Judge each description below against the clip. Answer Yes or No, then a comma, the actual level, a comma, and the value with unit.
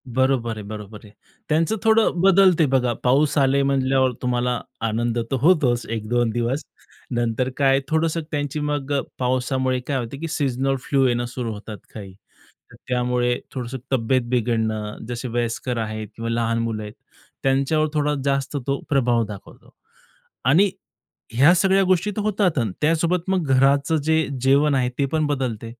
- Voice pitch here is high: No, low, 130 Hz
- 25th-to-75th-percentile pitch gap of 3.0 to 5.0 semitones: Yes, average, 3.9 semitones